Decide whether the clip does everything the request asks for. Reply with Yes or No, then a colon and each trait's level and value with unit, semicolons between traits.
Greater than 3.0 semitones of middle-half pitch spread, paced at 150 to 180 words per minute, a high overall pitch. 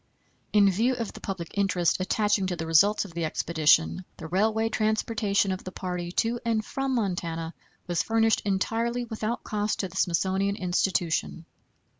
Yes: average, 3.8 semitones; average, 160 wpm; high, 195 Hz